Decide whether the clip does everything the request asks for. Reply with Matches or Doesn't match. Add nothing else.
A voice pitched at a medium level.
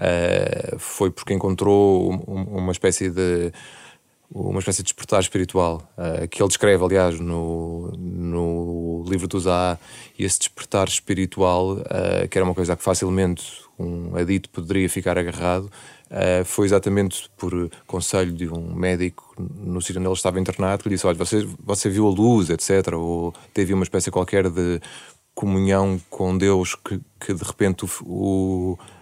Doesn't match